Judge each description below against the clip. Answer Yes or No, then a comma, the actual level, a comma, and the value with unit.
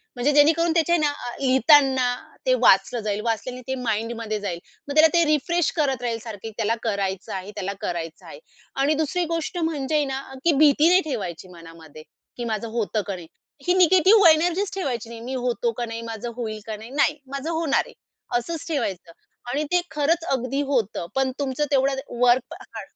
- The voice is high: Yes, very high, 260 Hz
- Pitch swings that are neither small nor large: No, wide, 5.7 semitones